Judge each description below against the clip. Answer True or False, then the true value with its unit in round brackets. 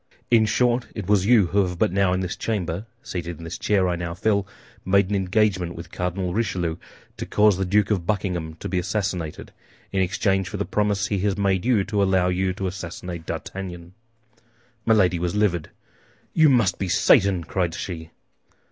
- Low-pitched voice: True (95 Hz)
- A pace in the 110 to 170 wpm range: False (185 wpm)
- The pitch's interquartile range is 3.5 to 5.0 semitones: False (2.6 semitones)